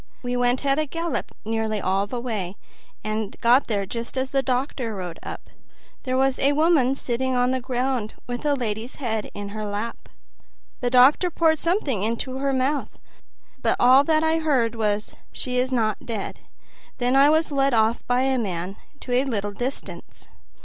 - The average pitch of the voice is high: Yes, very high, 250 Hz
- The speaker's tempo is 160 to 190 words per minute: Yes, average, 175 wpm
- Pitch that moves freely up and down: No, average, 3.6 semitones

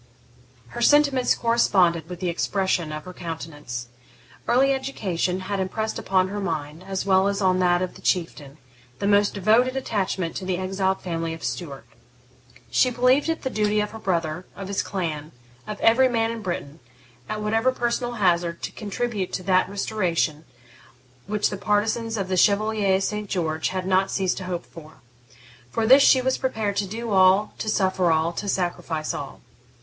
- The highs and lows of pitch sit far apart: No, average, 3.9 semitones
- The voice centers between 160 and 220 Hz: Yes, high, 190 Hz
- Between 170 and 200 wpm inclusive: Yes, average, 175 wpm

